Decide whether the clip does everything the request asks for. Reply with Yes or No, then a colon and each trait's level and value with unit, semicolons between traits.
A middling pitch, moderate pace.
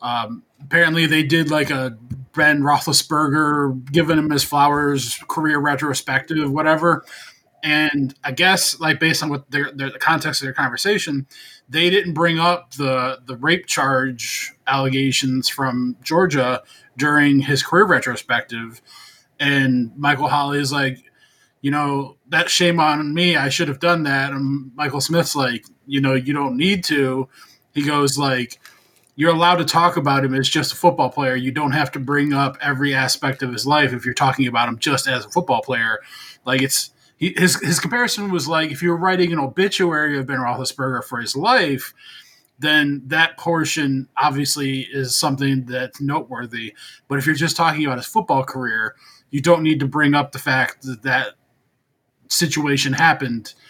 Yes: medium, 145 Hz; average, 170 wpm